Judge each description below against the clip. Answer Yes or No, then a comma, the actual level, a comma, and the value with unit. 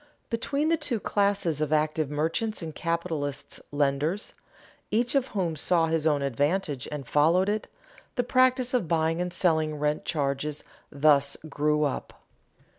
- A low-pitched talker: No, medium, 160 Hz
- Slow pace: No, average, 145 wpm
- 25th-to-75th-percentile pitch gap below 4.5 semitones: No, average, 5.2 semitones